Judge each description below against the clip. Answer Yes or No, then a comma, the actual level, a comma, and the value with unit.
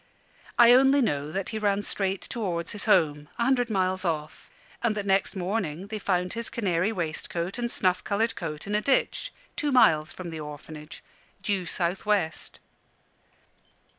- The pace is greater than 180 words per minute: No, average, 165 wpm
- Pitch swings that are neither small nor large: Yes, average, 4.6 semitones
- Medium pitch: No, high, 195 Hz